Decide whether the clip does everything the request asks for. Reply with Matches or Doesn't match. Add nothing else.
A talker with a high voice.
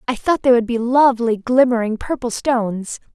Matches